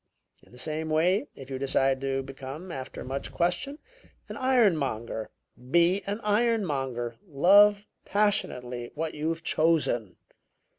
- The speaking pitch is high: No, medium, 155 Hz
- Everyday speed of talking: No, slow, 120 wpm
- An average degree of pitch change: No, wide, 6.5 semitones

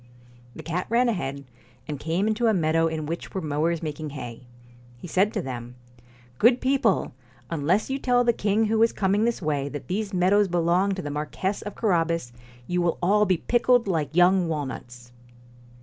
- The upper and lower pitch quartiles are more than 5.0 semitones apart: Yes, wide, 5.6 semitones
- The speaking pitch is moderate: Yes, medium, 175 Hz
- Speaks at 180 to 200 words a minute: Yes, average, 185 wpm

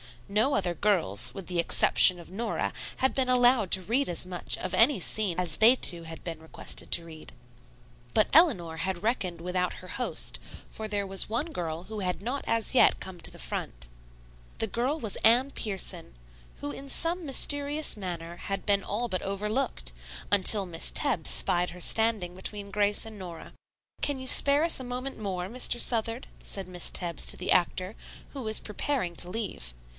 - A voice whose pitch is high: Yes, high, 200 Hz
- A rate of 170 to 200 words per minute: Yes, average, 185 wpm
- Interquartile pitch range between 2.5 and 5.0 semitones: No, wide, 5.4 semitones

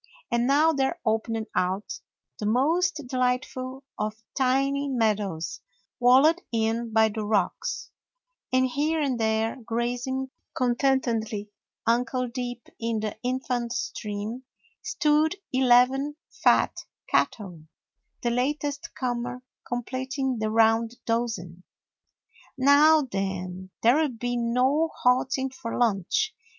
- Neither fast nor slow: No, slow, 110 wpm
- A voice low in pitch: No, high, 245 Hz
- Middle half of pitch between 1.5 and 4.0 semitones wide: Yes, average, 3.1 semitones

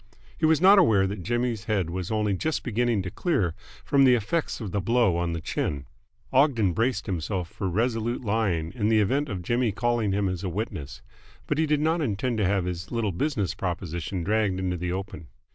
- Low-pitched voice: Yes, low, 105 Hz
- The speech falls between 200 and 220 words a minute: Yes, fast, 205 wpm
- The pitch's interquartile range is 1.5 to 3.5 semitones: No, average, 4.8 semitones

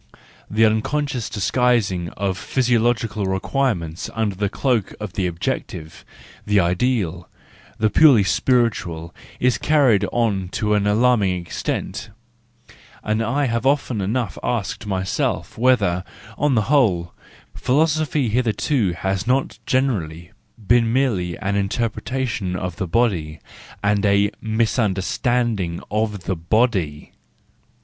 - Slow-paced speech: Yes, slow, 115 wpm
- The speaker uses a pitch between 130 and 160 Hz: No, low, 110 Hz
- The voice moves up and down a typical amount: Yes, average, 4.6 semitones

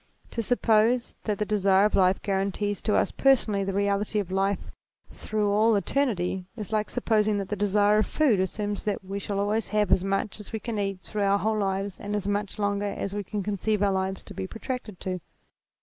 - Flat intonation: Yes, narrow, 1.4 semitones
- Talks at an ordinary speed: No, fast, 215 wpm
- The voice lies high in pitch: Yes, high, 205 Hz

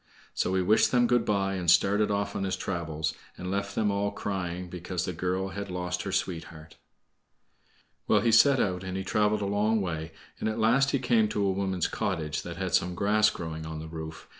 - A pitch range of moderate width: Yes, average, 3.0 semitones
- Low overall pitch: Yes, very low, 95 Hz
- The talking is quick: Yes, fast, 215 wpm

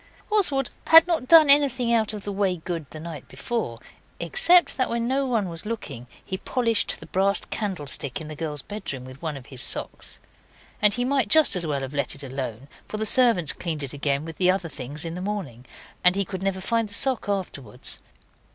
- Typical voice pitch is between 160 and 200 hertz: Yes, high, 190 Hz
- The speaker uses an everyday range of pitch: No, wide, 8.1 semitones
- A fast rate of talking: Yes, fast, 210 wpm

